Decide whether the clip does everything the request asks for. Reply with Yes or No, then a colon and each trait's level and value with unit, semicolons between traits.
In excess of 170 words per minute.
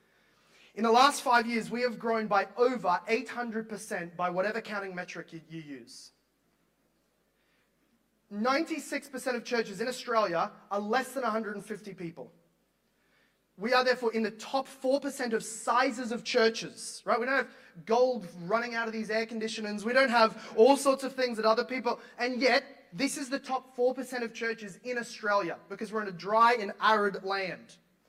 No: average, 165 wpm